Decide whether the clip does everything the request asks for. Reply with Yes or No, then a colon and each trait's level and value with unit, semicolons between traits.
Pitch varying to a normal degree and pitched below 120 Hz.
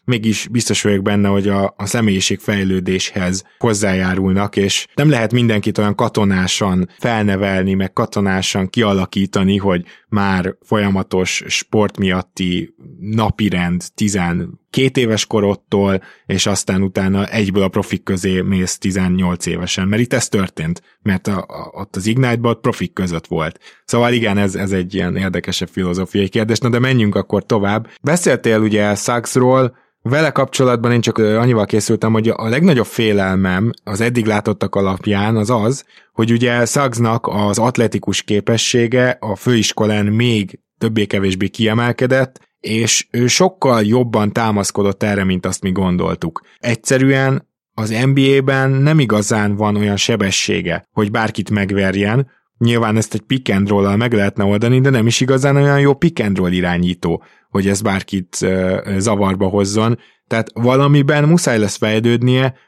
Yes: average, 3.4 semitones; low, 105 Hz